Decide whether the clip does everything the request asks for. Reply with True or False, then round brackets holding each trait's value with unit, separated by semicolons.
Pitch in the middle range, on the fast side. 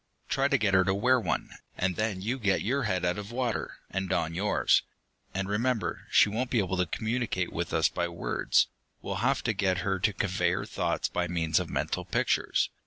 False (100 Hz; 210 wpm)